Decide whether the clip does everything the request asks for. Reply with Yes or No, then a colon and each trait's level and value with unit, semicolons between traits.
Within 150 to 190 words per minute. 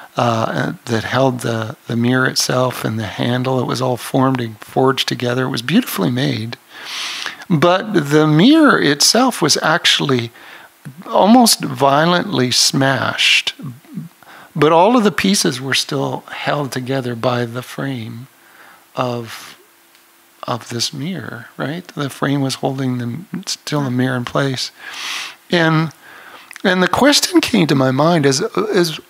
No: average, 140 wpm